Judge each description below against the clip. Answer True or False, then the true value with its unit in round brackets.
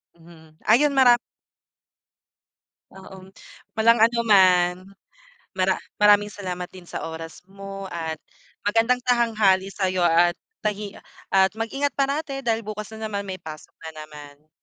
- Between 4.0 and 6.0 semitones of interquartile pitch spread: True (4.3 semitones)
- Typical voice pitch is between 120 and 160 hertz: False (195 Hz)